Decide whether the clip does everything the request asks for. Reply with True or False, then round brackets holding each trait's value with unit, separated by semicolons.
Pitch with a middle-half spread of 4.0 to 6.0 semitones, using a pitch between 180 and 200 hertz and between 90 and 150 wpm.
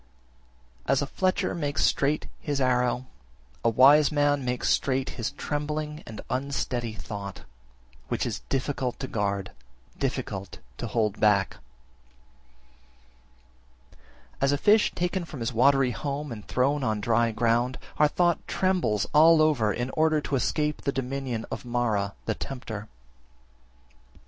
False (4.4 semitones; 130 Hz; 140 wpm)